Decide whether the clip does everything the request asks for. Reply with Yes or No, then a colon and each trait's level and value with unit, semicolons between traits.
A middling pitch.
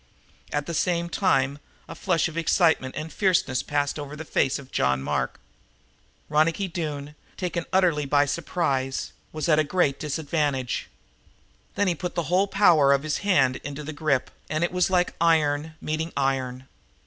Yes: medium, 155 Hz